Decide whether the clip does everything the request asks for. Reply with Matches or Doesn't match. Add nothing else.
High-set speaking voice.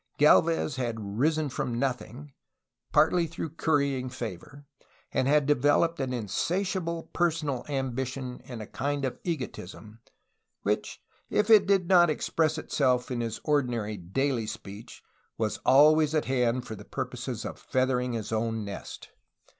Doesn't match